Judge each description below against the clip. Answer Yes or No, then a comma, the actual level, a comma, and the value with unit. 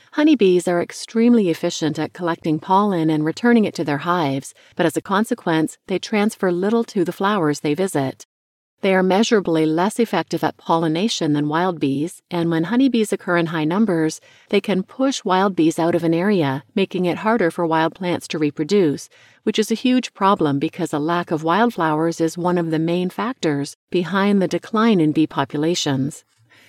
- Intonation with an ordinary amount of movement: Yes, average, 3.9 semitones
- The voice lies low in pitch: No, medium, 175 Hz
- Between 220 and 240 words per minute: No, average, 180 wpm